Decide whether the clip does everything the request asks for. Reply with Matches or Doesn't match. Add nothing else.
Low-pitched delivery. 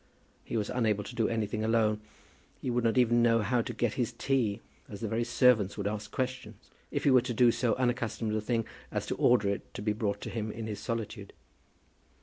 Matches